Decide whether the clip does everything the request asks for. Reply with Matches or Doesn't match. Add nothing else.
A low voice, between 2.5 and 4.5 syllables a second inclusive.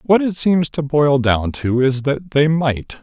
Doesn't match